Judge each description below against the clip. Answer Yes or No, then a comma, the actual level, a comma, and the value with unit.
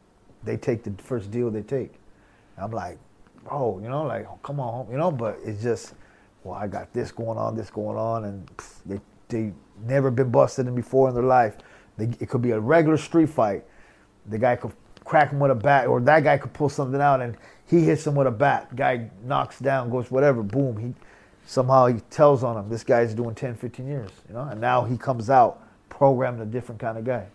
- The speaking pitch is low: Yes, low, 125 Hz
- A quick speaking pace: Yes, fast, 225 wpm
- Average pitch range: Yes, average, 3.4 semitones